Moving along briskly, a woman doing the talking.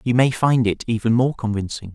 No: fast, 215 wpm; male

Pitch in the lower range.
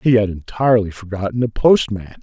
Yes: low, 110 Hz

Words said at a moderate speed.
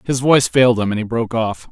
No: fast, 280 wpm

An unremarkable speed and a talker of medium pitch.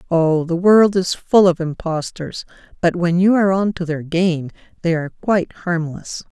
Yes: average, 180 wpm; medium, 175 Hz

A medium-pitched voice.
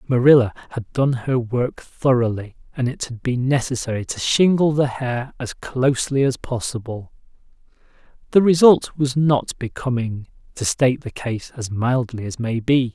No: low, 125 Hz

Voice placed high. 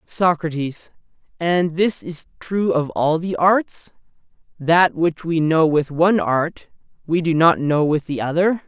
No: medium, 165 Hz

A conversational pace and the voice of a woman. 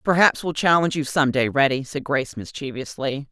Yes: average, 180 wpm; female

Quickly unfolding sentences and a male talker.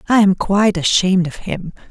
No: average, 190 wpm; male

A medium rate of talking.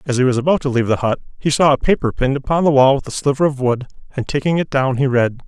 No: fast, 295 wpm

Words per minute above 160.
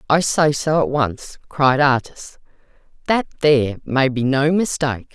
No: average, 150 wpm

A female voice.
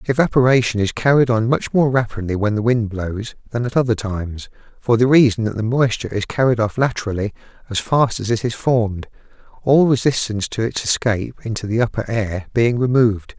No: male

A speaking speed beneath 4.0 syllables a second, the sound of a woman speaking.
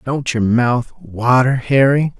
No: 3.5 syllables/s; male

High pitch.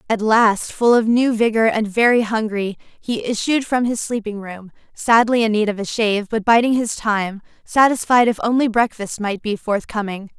Yes: high, 220 Hz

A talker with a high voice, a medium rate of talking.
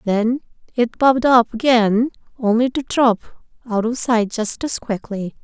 Yes: high, 235 Hz; average, 155 wpm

